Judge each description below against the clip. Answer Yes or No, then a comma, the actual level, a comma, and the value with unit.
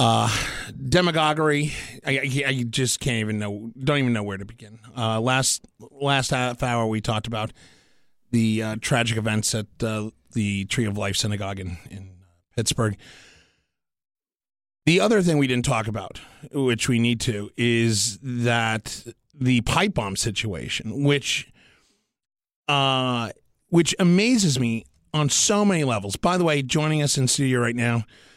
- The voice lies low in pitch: Yes, low, 120 Hz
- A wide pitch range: No, average, 4.2 semitones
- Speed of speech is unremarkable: Yes, average, 150 wpm